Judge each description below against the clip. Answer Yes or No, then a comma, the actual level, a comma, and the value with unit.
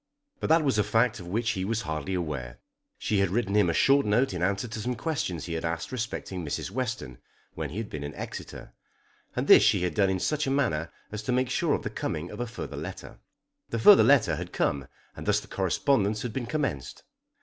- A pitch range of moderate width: No, wide, 6.4 semitones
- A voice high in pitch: No, low, 105 Hz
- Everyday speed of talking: No, fast, 230 wpm